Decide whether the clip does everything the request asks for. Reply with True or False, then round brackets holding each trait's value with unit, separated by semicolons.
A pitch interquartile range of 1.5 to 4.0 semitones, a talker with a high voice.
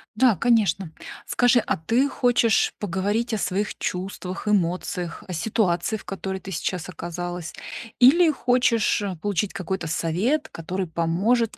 False (4.7 semitones; 195 Hz)